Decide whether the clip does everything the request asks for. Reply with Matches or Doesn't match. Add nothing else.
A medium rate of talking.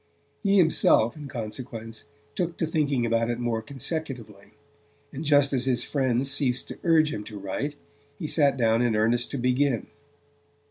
Matches